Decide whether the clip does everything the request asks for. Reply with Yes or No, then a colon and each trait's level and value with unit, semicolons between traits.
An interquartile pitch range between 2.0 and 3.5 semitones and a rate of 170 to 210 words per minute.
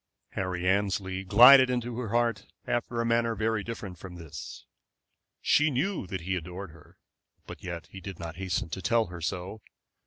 No: average, 4.5 semitones; average, 175 wpm